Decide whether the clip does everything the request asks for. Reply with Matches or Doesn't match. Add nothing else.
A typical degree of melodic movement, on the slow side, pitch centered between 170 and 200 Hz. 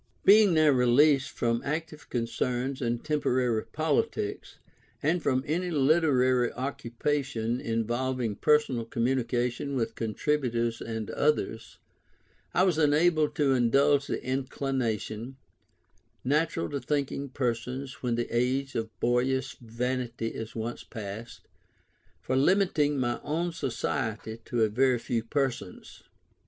Doesn't match